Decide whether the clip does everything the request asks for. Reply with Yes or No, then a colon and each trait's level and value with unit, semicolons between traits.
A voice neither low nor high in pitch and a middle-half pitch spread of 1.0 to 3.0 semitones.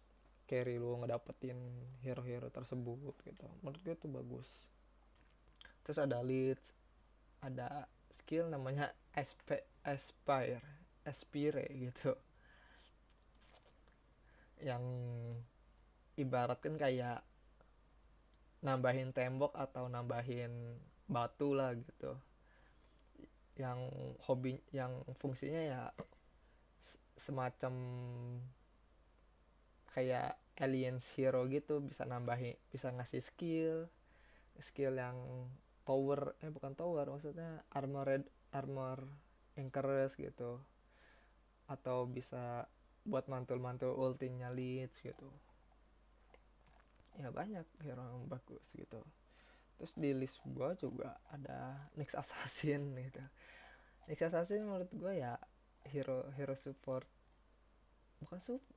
No: low, 130 Hz; narrow, 2.4 semitones